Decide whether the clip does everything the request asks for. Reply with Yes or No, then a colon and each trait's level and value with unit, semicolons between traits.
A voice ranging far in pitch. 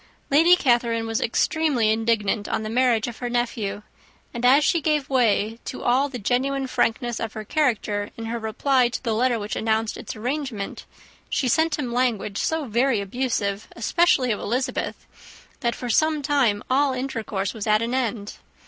No: average, 3.3 semitones